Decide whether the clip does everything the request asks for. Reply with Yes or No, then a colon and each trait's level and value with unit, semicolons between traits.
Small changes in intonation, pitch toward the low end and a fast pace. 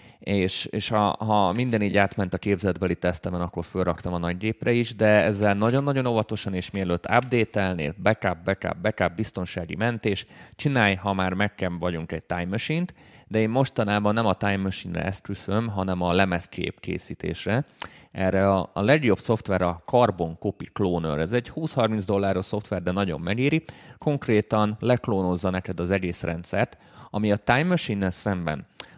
No: average, 3.2 semitones; low, 100 Hz; fast, 160 wpm